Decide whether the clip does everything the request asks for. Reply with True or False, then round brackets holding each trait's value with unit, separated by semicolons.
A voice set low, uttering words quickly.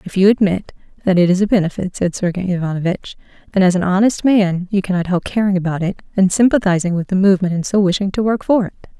False (190 Hz; 225 wpm)